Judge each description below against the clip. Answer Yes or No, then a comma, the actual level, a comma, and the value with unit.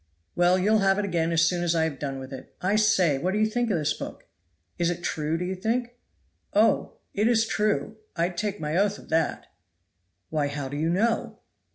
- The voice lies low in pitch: No, medium, 175 Hz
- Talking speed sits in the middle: No, fast, 220 wpm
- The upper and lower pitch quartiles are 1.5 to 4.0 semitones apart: No, average, 4.6 semitones